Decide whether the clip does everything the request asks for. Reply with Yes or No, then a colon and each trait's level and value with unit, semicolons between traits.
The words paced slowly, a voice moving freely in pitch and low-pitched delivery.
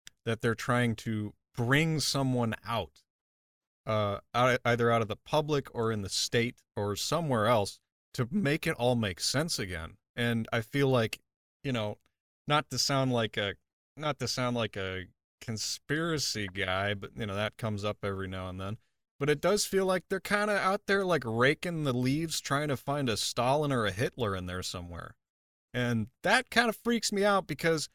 No: average, 190 wpm; wide, 5.7 semitones; low, 120 Hz